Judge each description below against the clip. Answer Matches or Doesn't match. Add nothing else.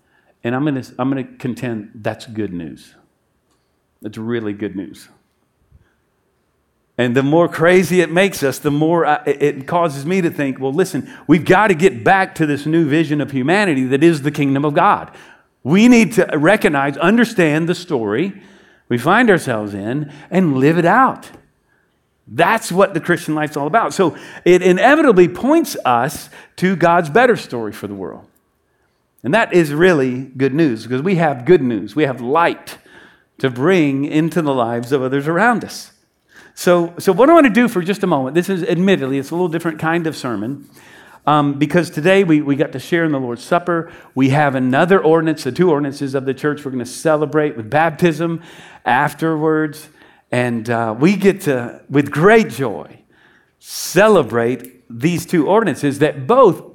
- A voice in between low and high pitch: Matches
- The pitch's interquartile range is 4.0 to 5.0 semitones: Matches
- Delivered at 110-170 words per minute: Doesn't match